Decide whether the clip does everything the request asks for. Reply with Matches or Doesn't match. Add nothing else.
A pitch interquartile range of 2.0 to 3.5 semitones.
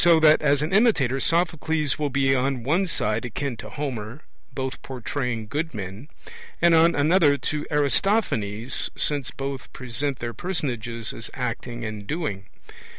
Doesn't match